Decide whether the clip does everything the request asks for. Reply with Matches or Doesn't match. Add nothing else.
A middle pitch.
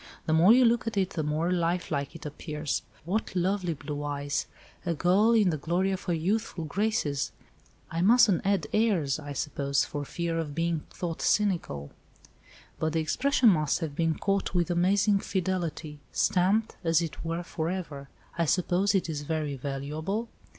Matches